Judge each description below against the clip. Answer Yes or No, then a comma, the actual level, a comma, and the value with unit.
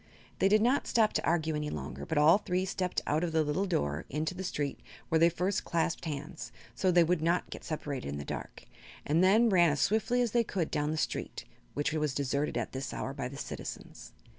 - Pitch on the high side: No, medium, 160 Hz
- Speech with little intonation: No, average, 4.0 semitones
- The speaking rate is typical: No, fast, 225 wpm